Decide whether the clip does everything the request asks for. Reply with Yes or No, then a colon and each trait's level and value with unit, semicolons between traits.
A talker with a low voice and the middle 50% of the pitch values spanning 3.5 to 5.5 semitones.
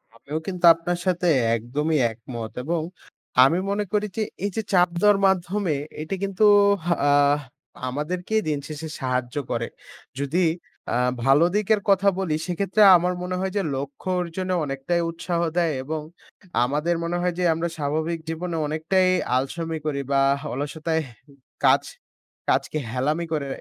No: medium, 165 Hz; average, 4.1 semitones